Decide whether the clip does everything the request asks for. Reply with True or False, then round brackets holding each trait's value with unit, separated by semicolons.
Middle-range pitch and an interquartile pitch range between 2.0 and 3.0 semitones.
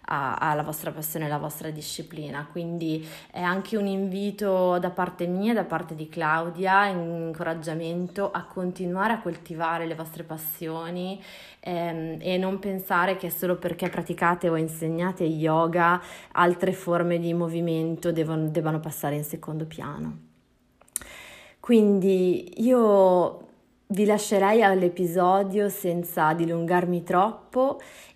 True (175 Hz; 2.7 semitones)